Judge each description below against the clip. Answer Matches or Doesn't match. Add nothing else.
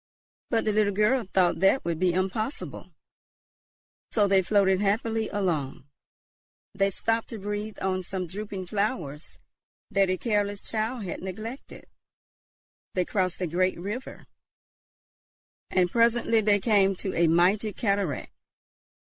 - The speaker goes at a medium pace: Doesn't match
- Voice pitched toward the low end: Doesn't match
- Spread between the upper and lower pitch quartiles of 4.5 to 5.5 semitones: Doesn't match